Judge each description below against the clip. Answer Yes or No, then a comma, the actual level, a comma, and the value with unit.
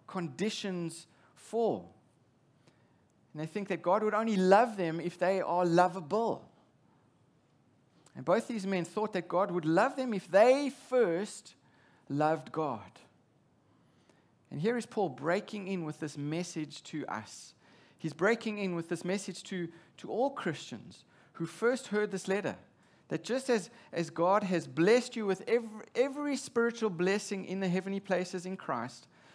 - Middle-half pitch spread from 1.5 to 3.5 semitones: No, average, 4.5 semitones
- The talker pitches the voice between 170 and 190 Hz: Yes, medium, 185 Hz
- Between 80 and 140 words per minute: No, average, 155 wpm